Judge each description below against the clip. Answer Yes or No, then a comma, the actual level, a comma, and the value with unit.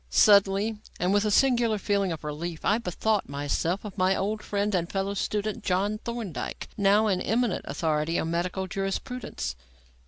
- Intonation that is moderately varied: Yes, average, 3.4 semitones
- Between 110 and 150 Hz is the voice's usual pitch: No, high, 195 Hz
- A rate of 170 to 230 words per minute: No, average, 160 wpm